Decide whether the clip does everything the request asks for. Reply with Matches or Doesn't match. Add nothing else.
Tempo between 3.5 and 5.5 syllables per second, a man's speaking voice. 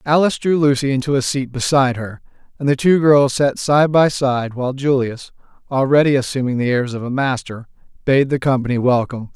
Doesn't match